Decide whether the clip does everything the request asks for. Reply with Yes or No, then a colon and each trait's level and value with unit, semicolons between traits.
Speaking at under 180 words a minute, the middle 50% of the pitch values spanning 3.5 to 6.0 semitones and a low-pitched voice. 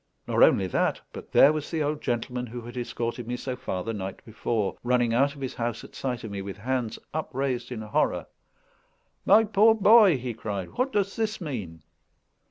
No: average, 195 wpm; average, 4.9 semitones; low, 125 Hz